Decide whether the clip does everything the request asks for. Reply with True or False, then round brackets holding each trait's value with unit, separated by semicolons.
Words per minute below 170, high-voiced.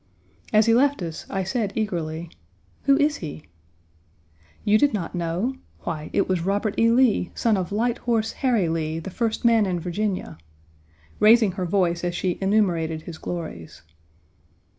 True (160 wpm; 195 Hz)